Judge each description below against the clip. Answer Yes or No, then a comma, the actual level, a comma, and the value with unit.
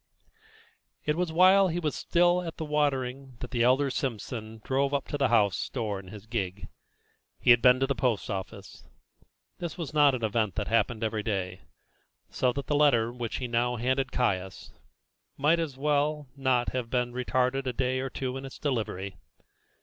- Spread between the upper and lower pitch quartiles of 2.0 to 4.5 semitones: Yes, average, 3.8 semitones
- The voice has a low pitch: Yes, low, 130 Hz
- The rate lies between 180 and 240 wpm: Yes, average, 190 wpm